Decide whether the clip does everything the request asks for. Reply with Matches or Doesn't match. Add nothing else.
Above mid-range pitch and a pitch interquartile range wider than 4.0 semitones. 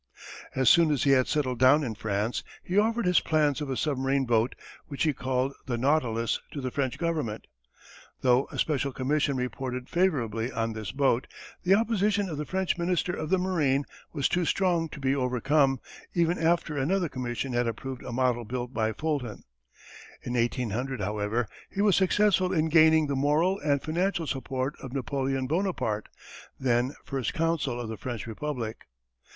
Doesn't match